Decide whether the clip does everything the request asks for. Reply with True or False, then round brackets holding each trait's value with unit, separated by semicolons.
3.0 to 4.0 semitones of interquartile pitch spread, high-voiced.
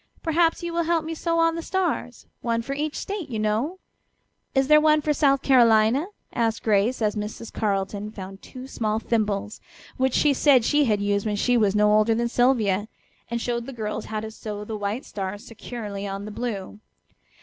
False (4.7 semitones; 230 Hz)